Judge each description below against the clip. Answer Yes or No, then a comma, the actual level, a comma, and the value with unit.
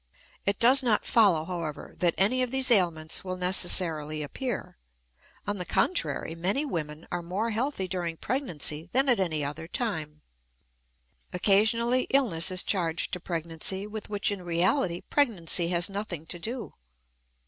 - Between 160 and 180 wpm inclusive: No, average, 150 wpm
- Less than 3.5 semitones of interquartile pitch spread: No, average, 5.2 semitones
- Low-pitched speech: No, medium, 185 Hz